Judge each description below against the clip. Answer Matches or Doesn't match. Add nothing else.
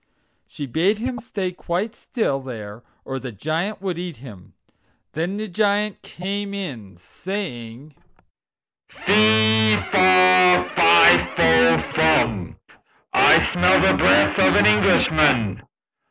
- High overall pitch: Doesn't match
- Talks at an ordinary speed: Doesn't match